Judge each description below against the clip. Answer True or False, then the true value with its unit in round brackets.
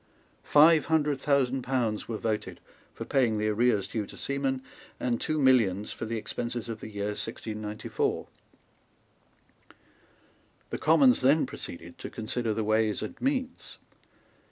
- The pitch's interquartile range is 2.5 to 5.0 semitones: True (4.3 semitones)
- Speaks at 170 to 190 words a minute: False (135 wpm)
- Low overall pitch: True (120 Hz)